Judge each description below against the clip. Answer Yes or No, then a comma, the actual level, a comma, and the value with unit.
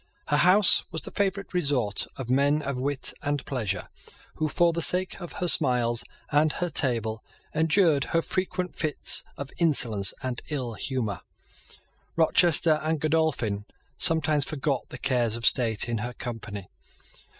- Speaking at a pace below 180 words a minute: Yes, average, 150 wpm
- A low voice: No, medium, 145 Hz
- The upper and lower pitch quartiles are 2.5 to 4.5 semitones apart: No, average, 5.1 semitones